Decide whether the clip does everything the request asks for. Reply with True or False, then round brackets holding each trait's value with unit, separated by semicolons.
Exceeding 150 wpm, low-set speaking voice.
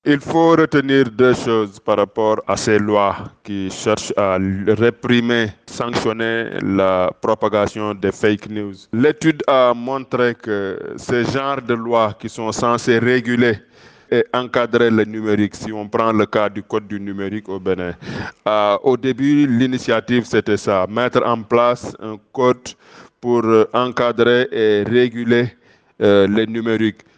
False (145 wpm; 115 Hz)